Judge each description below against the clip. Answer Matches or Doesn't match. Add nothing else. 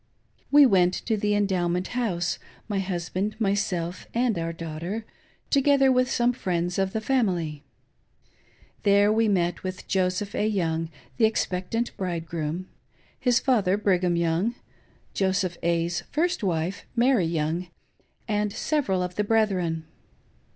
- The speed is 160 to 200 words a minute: Doesn't match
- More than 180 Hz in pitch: Matches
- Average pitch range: Matches